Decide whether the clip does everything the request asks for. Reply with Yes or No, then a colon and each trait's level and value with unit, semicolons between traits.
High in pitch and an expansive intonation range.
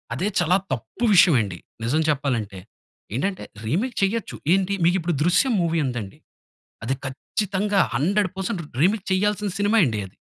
No: medium, 180 Hz; wide, 7.0 semitones